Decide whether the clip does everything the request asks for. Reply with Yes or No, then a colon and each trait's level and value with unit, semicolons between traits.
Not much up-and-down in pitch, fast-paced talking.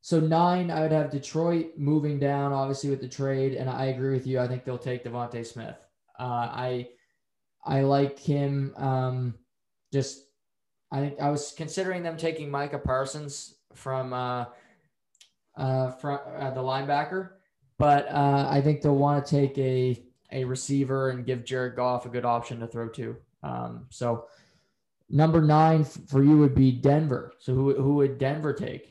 No: narrow, 2.3 semitones; average, 170 wpm